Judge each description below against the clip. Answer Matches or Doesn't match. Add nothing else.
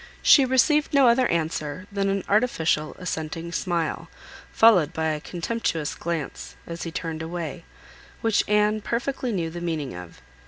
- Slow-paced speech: Doesn't match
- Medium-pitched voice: Matches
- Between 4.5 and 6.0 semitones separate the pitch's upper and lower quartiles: Matches